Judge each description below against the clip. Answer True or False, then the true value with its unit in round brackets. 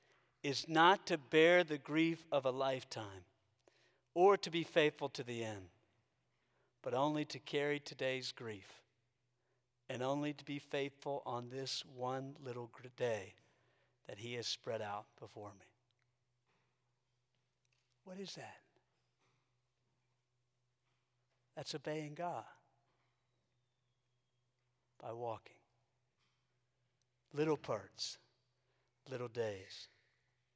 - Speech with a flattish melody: True (2.3 semitones)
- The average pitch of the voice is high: False (125 Hz)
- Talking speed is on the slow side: True (100 wpm)